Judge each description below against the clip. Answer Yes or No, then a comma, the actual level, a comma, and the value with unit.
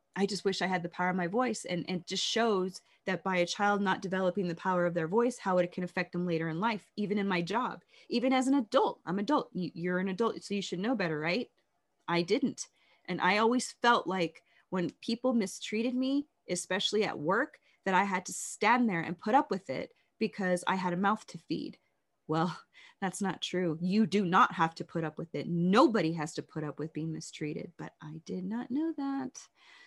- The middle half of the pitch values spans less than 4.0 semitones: No, average, 4.3 semitones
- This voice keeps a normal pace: No, fast, 225 wpm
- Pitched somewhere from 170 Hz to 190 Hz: Yes, medium, 185 Hz